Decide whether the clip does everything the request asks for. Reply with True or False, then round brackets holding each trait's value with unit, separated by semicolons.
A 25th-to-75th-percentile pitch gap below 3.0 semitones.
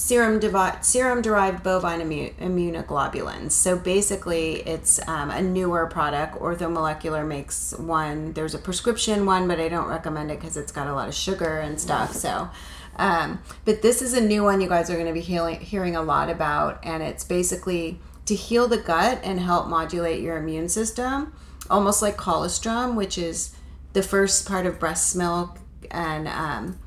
False (3.4 semitones)